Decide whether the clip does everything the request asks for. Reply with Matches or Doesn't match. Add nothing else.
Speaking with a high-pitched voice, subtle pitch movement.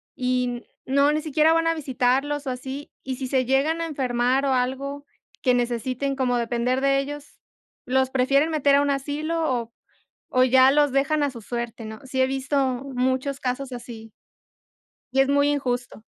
Matches